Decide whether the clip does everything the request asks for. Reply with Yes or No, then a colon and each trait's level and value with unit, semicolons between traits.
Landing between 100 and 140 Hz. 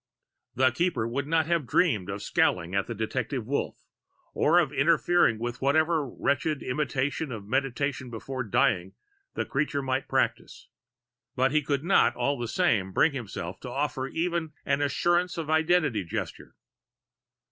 Yes: low, 135 Hz